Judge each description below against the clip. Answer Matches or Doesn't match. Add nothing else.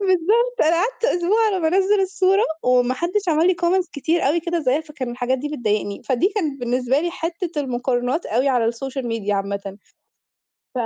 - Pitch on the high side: Matches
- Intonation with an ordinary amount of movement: Doesn't match